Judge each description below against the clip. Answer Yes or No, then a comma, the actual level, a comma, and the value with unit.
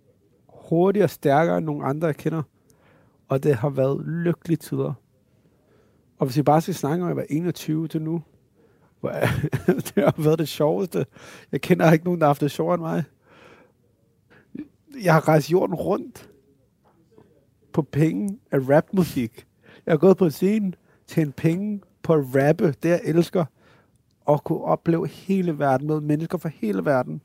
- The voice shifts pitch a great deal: No, average, 3.3 semitones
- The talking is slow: No, average, 165 wpm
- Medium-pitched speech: Yes, medium, 160 Hz